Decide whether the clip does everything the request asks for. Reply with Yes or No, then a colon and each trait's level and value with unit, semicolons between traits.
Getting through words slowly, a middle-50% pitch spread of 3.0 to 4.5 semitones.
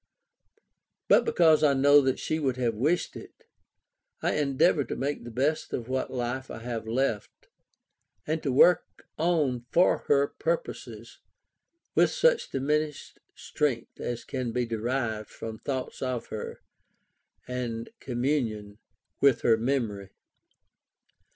Yes: slow, 130 wpm; average, 3.8 semitones